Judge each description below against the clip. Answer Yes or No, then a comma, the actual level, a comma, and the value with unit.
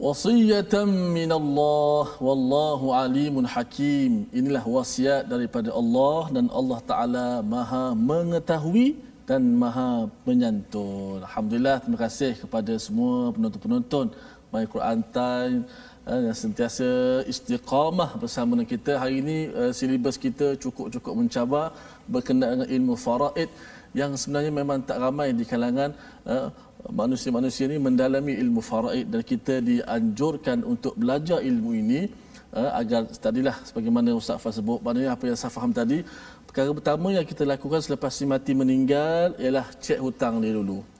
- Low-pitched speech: No, medium, 165 Hz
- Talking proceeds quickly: Yes, fast, 130 wpm